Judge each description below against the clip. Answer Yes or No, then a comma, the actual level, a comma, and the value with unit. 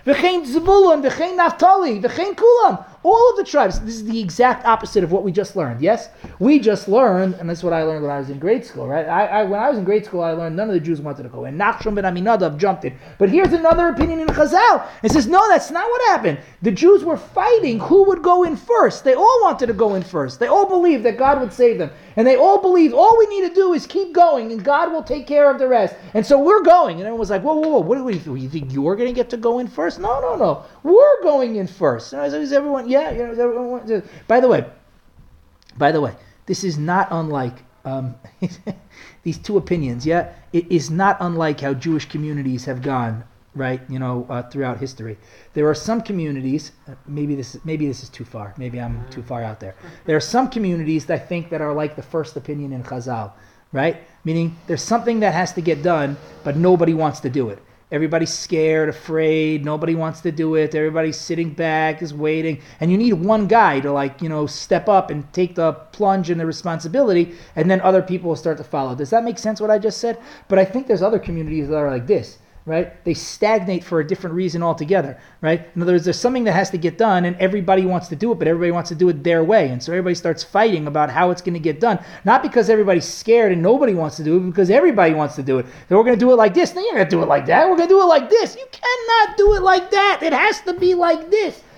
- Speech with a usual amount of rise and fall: No, wide, 7.7 semitones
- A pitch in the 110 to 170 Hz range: No, medium, 180 Hz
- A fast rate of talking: Yes, fast, 255 wpm